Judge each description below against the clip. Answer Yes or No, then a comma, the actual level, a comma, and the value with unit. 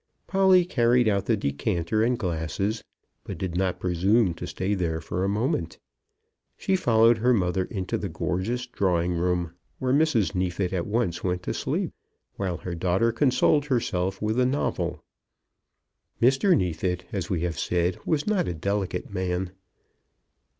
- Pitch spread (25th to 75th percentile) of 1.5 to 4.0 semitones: No, average, 5.0 semitones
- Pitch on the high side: No, very low, 95 Hz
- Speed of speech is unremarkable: Yes, average, 155 wpm